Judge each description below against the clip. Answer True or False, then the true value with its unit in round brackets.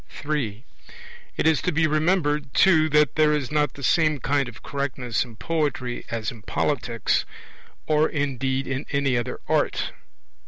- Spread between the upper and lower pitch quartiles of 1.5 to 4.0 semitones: True (3.3 semitones)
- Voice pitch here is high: False (145 Hz)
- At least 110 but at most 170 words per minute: True (150 wpm)